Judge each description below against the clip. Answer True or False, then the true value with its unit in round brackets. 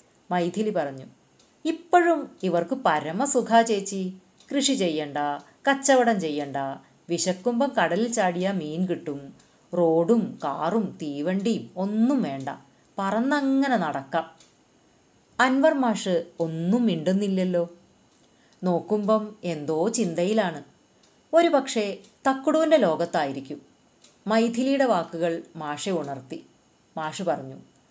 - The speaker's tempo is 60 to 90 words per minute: True (85 wpm)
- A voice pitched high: True (195 Hz)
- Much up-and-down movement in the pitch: True (6.1 semitones)